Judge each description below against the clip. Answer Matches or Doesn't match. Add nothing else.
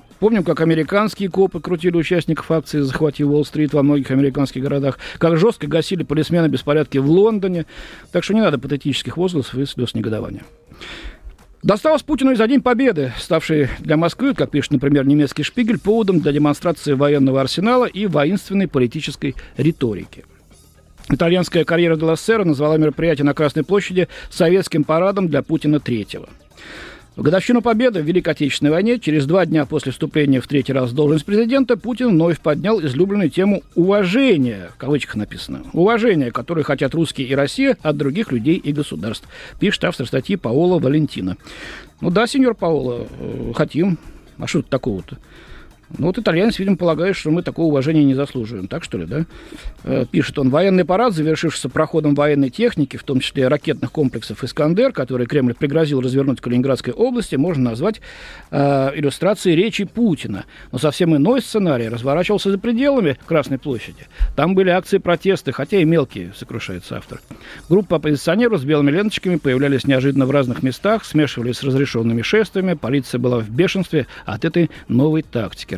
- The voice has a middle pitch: Matches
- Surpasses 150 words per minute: Matches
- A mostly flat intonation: Doesn't match